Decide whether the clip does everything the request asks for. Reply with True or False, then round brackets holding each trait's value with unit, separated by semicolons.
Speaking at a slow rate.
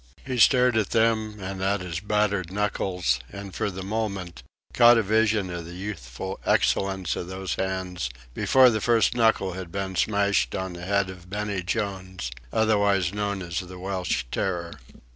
False (165 wpm)